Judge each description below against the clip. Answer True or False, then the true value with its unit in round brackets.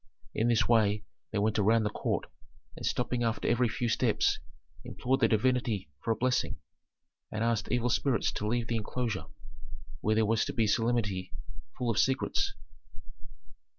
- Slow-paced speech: False (165 wpm)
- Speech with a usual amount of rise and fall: False (2.0 semitones)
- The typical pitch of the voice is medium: False (115 Hz)